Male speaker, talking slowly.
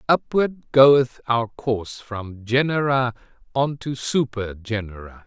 Yes: male; slow, 115 wpm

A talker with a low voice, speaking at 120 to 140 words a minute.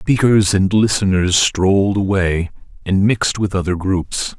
Yes: low, 100 Hz; slow, 135 wpm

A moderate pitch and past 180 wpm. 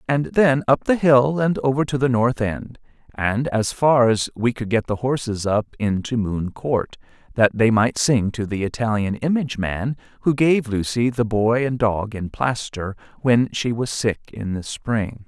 No: low, 115 Hz; average, 190 wpm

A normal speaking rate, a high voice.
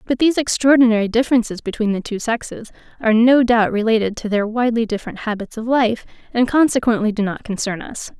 Yes: average, 185 wpm; high, 225 Hz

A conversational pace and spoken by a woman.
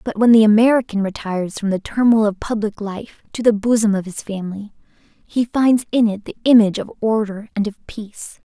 Yes: average, 195 wpm; female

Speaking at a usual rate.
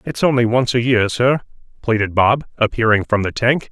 Yes: average, 195 wpm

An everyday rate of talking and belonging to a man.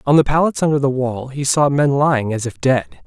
No: fast, 255 wpm; male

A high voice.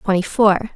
Yes: high, 200 Hz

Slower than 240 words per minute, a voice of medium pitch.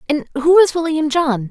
No: average, 200 wpm; very high, 295 Hz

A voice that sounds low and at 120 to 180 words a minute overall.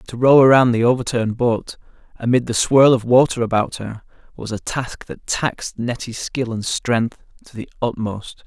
Yes: low, 120 Hz; average, 175 wpm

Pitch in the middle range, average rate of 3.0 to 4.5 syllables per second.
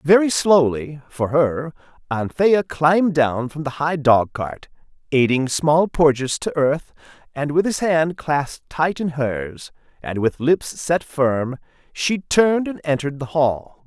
Yes: medium, 150 Hz; 3.9 syllables/s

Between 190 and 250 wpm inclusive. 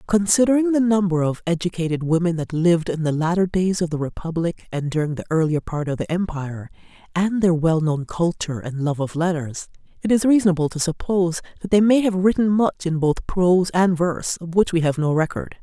Yes: fast, 205 wpm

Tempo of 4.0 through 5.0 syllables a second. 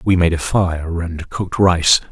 Yes: 4.1 syllables/s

